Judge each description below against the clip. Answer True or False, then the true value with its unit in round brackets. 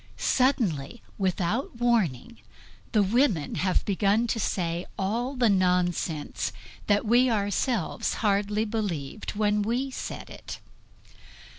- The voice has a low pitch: False (210 Hz)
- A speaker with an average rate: False (110 wpm)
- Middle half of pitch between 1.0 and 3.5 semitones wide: False (4.3 semitones)